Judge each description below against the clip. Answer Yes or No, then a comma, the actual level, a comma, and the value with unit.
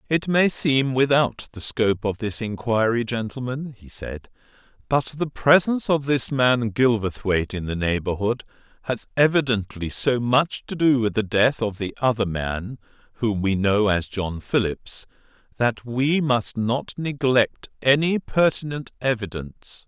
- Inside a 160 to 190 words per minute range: No, average, 150 wpm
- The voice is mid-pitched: No, low, 120 Hz